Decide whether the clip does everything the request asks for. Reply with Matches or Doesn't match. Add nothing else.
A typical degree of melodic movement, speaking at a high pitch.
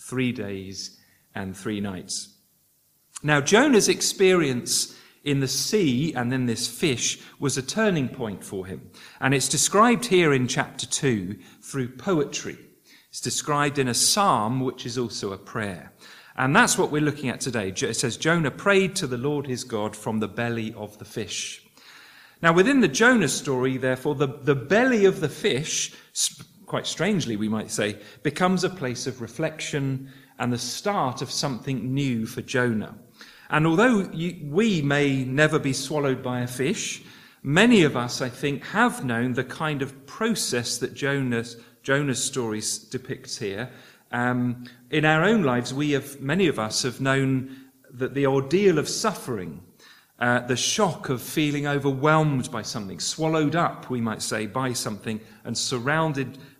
Doesn't match